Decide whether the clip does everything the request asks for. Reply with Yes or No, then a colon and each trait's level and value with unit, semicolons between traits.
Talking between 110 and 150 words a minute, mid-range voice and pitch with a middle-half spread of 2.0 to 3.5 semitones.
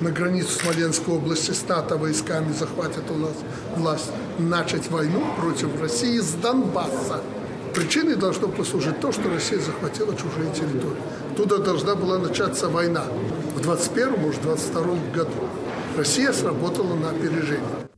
Yes: average, 125 wpm; medium, 165 Hz; average, 2.9 semitones